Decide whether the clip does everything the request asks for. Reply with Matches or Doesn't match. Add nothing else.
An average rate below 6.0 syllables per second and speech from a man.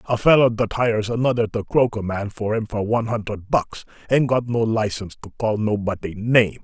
Matches